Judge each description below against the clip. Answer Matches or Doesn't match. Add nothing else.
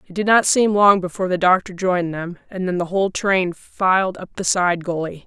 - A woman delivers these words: Matches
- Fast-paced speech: Matches